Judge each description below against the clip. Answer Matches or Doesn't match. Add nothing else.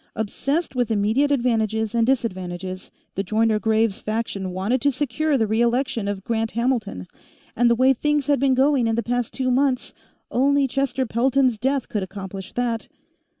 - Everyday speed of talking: Matches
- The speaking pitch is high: Matches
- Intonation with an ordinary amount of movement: Matches